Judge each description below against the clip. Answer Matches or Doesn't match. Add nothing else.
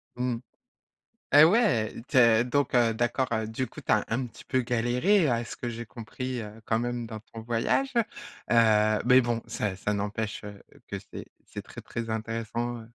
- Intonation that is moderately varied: Doesn't match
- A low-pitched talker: Matches